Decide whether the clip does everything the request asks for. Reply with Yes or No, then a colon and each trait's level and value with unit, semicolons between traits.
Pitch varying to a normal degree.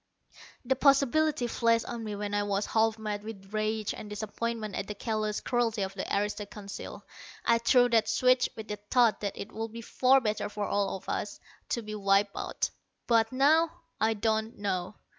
No: narrow, 2.3 semitones